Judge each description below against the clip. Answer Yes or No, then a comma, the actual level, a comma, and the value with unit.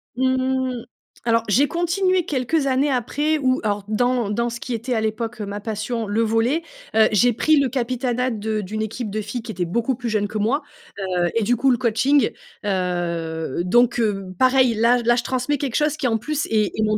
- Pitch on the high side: Yes, high, 235 Hz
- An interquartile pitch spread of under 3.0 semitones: No, average, 3.3 semitones